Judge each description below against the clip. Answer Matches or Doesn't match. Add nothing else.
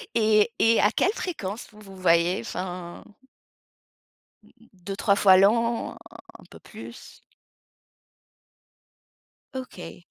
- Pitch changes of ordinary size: Matches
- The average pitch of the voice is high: Matches